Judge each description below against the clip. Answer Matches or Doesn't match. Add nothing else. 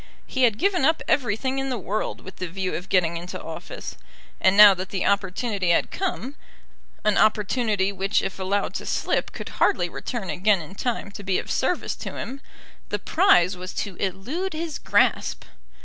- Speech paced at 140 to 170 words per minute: Doesn't match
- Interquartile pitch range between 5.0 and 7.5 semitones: Matches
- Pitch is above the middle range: Matches